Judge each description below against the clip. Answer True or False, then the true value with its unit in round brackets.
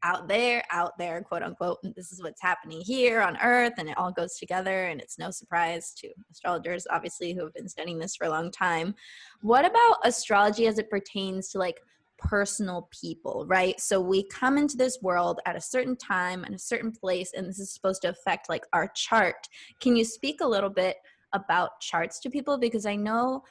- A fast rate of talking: True (210 wpm)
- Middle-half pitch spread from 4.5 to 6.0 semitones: True (4.9 semitones)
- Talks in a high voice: True (195 Hz)